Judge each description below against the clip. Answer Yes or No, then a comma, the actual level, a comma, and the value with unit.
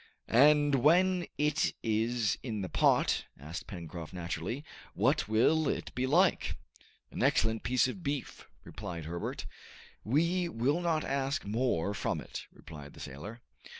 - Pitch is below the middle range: Yes, low, 120 Hz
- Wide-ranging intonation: Yes, wide, 7.9 semitones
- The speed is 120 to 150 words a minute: Yes, average, 140 wpm